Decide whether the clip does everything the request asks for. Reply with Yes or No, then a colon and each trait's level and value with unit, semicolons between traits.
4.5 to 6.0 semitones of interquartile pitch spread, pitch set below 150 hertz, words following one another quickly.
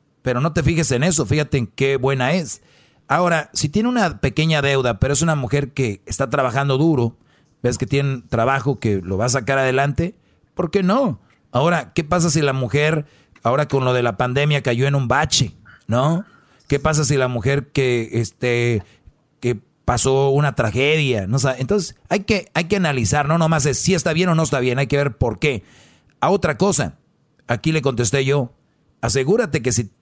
No: average, 4.0 semitones; medium, 140 Hz; fast, 200 wpm